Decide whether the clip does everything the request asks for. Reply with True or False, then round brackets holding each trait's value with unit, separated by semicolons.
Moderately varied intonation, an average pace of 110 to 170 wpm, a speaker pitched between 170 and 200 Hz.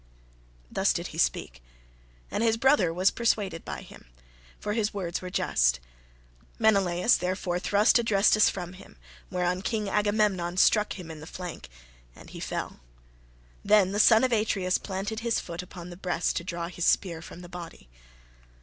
True (3.3 semitones; 165 wpm; 185 Hz)